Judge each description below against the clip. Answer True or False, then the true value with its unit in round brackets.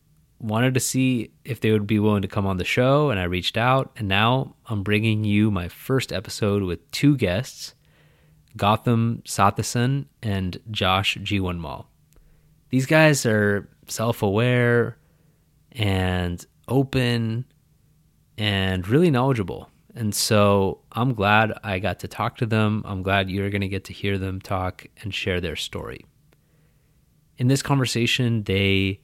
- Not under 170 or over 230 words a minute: False (145 wpm)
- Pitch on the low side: True (110 Hz)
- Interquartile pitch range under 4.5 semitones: False (4.9 semitones)